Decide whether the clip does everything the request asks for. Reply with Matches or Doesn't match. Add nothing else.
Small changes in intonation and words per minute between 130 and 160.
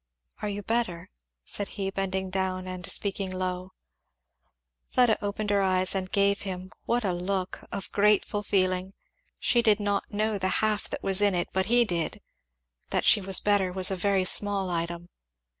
Doesn't match